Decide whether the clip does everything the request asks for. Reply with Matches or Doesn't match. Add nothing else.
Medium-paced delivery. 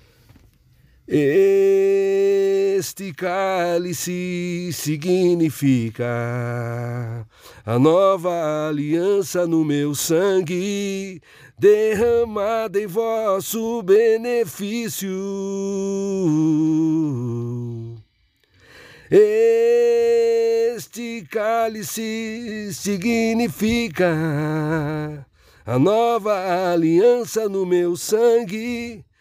Doesn't match